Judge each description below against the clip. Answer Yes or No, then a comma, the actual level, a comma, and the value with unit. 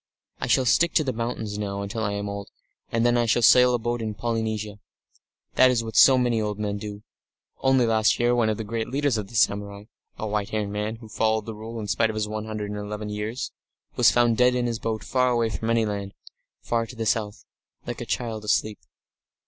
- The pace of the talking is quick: Yes, fast, 235 wpm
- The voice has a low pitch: Yes, low, 110 Hz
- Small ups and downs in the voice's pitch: Yes, narrow, 2.2 semitones